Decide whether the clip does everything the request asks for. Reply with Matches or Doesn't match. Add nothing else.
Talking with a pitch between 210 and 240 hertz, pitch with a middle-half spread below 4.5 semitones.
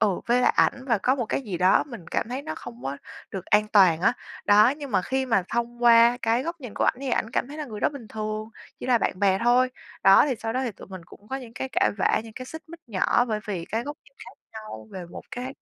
Matches